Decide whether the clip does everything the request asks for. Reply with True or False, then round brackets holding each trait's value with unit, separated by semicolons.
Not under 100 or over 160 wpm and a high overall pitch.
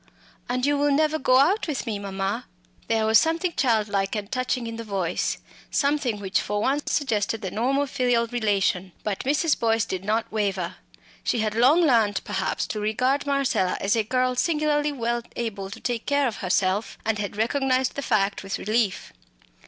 False (180 wpm; 230 Hz)